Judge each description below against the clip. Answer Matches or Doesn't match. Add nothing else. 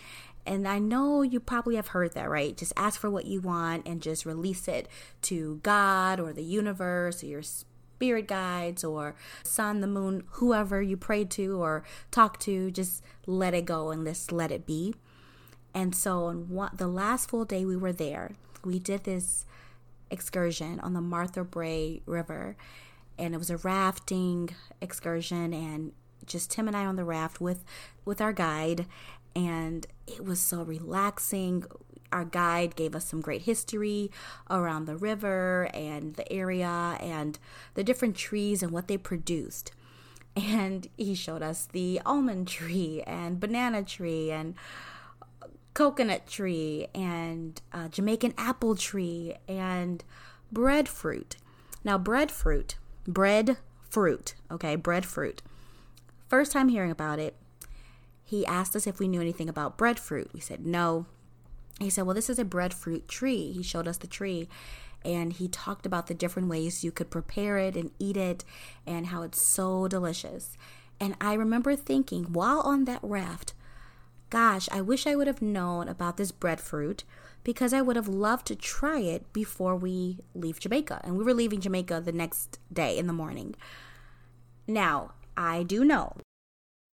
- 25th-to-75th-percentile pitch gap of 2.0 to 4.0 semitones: Matches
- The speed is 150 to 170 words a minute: Matches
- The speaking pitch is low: Doesn't match